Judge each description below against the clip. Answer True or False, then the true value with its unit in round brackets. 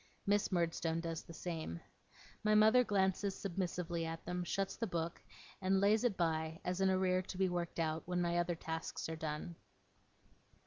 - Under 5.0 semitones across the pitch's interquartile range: True (2.6 semitones)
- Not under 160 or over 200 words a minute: True (175 wpm)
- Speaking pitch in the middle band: True (175 Hz)